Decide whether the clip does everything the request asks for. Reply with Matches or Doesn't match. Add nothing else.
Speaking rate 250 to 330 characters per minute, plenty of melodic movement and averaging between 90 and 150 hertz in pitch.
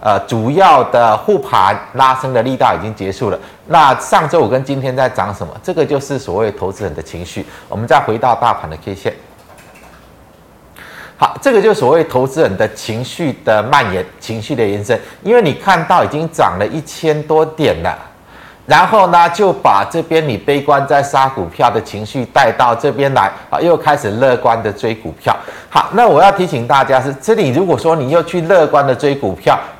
Matches